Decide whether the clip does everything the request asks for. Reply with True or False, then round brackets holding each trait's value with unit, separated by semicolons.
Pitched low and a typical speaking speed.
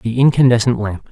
True (115 Hz; 160 wpm)